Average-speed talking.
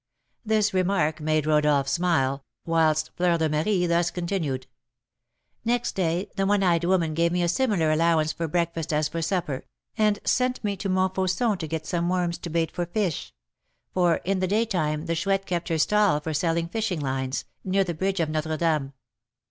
Yes: average, 185 wpm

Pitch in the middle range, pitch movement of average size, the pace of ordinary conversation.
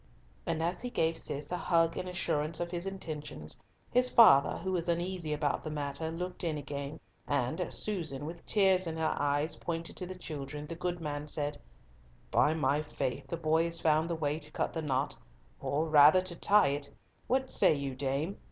Yes: medium, 160 Hz; average, 3.2 semitones; average, 195 wpm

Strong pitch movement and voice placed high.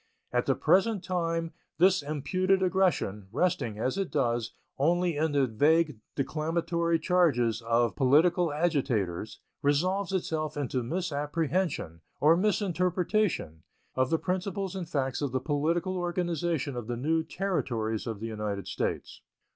No: wide, 5.7 semitones; medium, 160 Hz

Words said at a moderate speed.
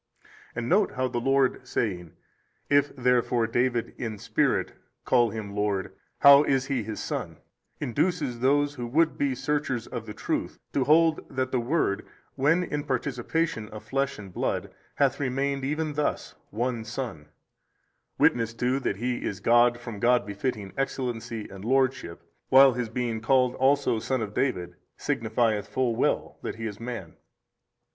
Yes: average, 155 wpm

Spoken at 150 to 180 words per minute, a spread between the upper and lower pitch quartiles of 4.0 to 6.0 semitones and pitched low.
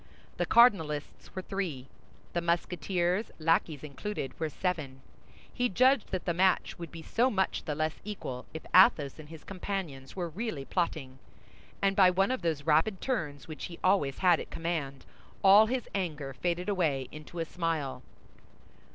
No: average, 160 wpm; average, 4.3 semitones; medium, 170 Hz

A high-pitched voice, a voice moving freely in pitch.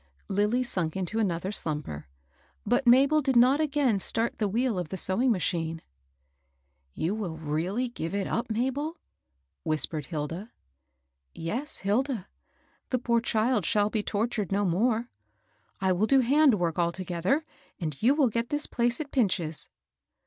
Yes: high, 205 Hz; wide, 6.7 semitones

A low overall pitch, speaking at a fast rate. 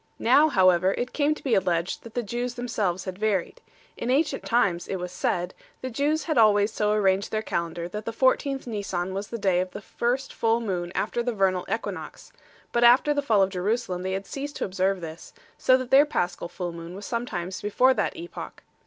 No: high, 210 Hz; fast, 210 wpm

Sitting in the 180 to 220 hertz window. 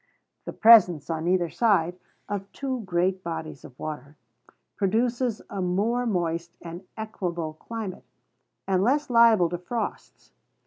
Yes: medium, 185 Hz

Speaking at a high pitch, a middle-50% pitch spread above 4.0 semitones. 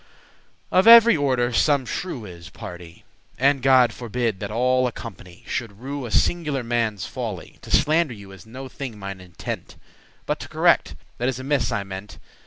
No: low, 120 Hz; average, 5.0 semitones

